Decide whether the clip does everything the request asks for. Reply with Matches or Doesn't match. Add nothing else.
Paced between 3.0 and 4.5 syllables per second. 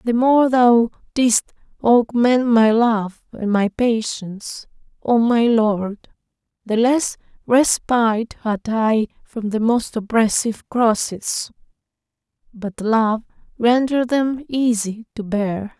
Matches